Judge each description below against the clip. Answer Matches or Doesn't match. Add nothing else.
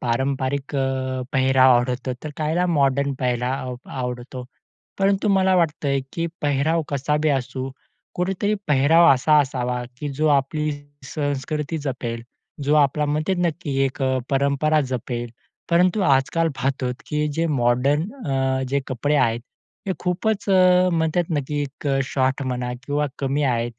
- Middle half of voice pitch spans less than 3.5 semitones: Matches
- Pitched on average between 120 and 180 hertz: Matches